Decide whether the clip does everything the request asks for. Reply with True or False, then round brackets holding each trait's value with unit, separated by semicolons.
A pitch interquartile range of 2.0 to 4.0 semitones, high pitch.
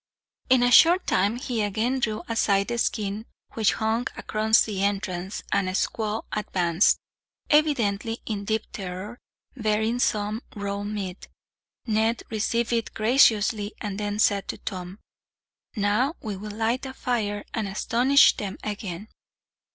True (2.4 semitones; 215 Hz)